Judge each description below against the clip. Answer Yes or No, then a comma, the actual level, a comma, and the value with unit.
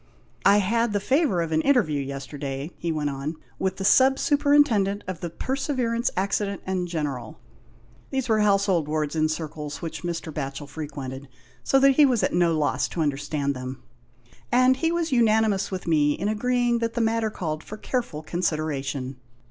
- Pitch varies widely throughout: Yes, wide, 7.4 semitones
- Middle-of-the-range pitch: Yes, medium, 180 Hz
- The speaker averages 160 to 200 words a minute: Yes, average, 180 wpm